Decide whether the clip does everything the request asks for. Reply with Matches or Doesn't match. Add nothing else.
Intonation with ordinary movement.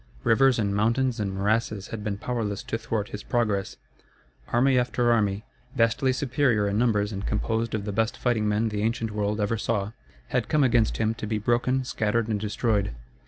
Doesn't match